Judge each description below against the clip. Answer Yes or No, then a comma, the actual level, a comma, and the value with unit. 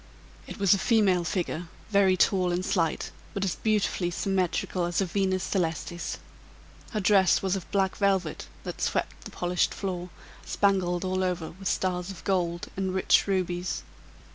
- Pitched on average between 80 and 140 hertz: No, medium, 185 Hz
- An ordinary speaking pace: Yes, average, 160 wpm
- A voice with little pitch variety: Yes, narrow, 1.8 semitones